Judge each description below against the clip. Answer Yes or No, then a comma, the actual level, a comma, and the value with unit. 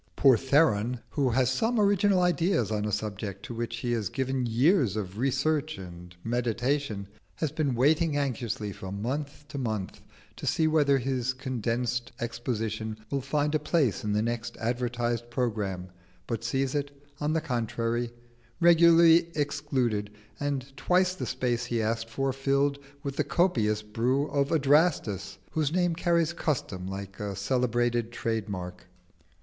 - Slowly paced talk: No, average, 150 wpm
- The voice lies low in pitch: Yes, low, 125 Hz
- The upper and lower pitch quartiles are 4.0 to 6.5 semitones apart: Yes, average, 4.6 semitones